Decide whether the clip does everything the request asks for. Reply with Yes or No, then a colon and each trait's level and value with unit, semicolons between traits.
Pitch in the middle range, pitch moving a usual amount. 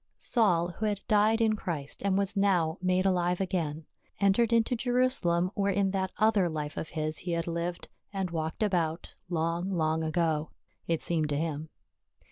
Yes: medium, 180 Hz; average, 3.7 semitones